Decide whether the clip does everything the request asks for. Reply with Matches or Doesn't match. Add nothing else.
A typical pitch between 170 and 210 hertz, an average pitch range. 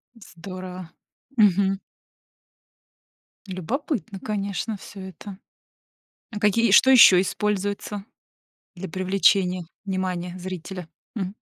Doesn't match